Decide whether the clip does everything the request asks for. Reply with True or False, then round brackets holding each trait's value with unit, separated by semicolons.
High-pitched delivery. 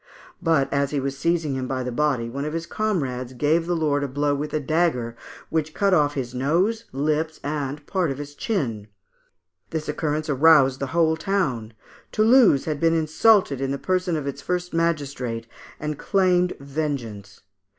False (150 Hz)